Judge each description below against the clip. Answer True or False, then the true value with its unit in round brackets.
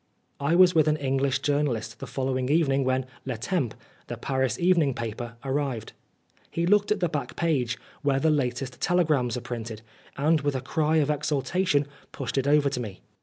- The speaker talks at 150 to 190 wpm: True (180 wpm)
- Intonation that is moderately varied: True (3.6 semitones)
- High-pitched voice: False (140 Hz)